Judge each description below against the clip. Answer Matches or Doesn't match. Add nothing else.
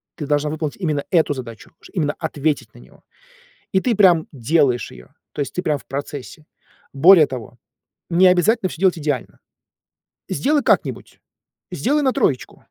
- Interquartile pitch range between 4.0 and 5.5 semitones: Matches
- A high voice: Doesn't match